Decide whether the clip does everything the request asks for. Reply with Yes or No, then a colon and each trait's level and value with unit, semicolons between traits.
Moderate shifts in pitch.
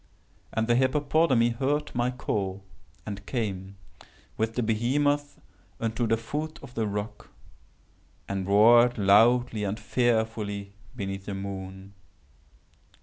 Yes: average, 3.7 semitones